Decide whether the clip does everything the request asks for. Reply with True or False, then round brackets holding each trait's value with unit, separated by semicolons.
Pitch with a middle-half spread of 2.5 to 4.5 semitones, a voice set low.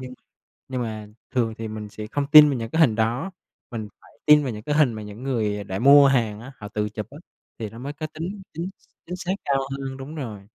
False (5.0 semitones; 125 Hz)